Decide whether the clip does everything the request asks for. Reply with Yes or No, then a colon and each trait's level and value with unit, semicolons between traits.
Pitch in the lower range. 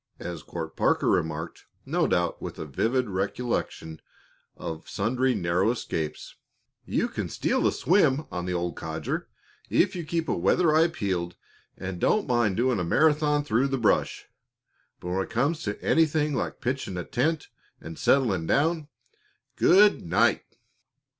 Yes: low, 115 Hz